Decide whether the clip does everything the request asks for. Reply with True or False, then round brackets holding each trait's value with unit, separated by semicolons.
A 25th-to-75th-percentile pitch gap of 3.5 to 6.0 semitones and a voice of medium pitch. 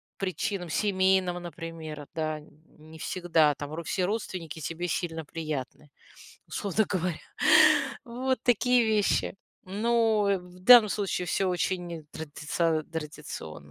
True (3.9 semitones; 175 Hz)